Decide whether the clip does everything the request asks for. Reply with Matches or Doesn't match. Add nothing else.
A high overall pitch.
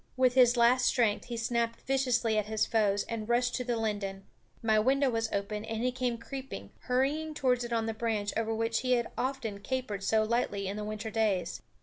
Matches